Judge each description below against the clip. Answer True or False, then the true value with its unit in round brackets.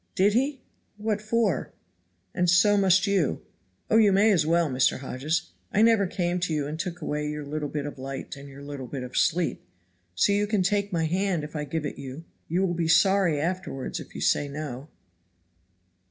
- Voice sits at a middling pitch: True (170 Hz)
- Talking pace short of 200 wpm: False (205 wpm)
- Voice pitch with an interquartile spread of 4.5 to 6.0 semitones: True (5.2 semitones)